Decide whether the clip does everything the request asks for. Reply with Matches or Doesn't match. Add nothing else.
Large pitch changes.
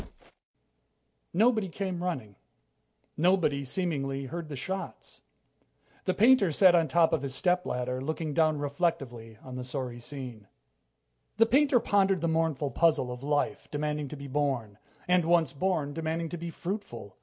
Doesn't match